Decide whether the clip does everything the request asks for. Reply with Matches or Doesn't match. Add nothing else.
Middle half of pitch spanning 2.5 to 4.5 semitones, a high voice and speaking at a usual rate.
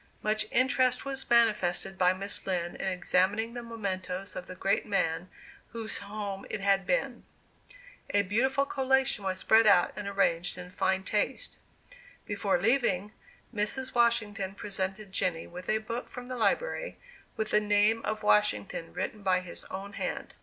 Matches